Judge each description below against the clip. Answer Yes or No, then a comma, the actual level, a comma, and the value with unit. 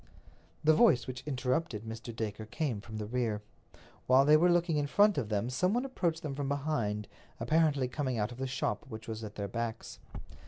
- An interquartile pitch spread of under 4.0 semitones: No, wide, 5.6 semitones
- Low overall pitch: Yes, low, 130 Hz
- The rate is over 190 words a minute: Yes, average, 200 wpm